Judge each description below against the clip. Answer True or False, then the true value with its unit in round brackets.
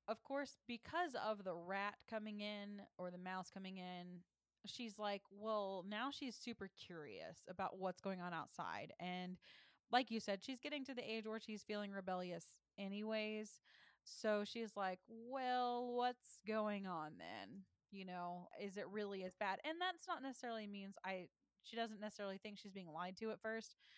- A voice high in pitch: True (210 Hz)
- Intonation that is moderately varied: True (3.2 semitones)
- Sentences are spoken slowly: False (175 wpm)